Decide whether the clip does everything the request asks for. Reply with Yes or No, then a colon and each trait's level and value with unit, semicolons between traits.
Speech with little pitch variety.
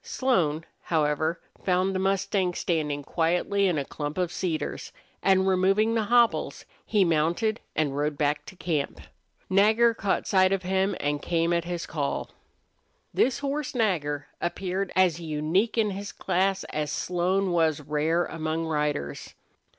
No: average, 3.9 semitones